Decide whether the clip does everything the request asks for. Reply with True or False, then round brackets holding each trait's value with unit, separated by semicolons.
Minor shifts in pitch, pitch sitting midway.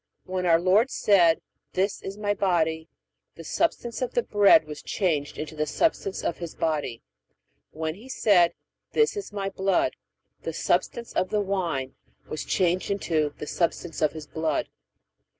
False (4.3 semitones; 180 Hz)